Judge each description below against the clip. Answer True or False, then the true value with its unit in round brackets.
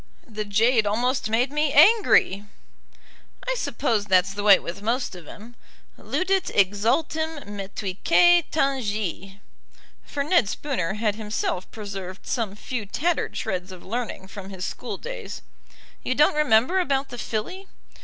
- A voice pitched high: True (220 Hz)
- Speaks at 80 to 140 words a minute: True (135 wpm)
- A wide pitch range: True (6.1 semitones)